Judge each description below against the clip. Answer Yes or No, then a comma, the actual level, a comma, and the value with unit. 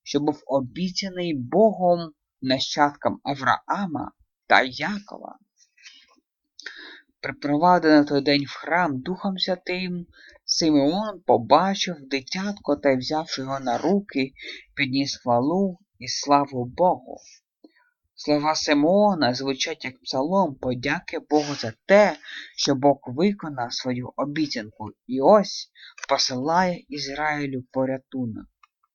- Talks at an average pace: No, slow, 95 wpm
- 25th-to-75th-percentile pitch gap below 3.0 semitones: No, average, 5.3 semitones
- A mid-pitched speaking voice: Yes, medium, 150 Hz